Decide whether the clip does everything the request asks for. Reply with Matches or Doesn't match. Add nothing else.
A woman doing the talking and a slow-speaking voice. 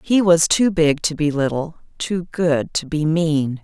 Doesn't match